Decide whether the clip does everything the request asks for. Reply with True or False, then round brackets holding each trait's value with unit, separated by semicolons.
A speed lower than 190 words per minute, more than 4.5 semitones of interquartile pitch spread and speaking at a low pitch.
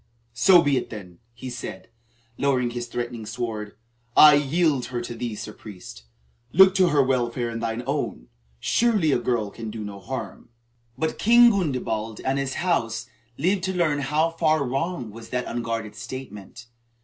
True (165 wpm; 5.1 semitones; 125 Hz)